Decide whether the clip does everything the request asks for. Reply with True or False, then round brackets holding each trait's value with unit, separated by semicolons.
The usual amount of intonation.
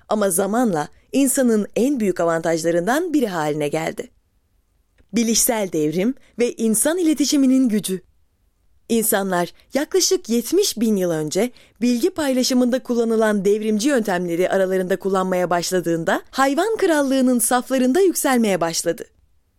False (7.2 semitones)